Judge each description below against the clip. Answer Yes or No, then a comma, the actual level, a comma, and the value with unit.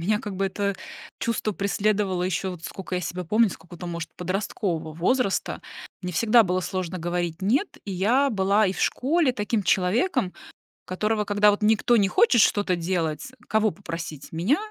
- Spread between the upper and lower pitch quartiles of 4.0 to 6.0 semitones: No, average, 3.2 semitones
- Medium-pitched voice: No, high, 195 Hz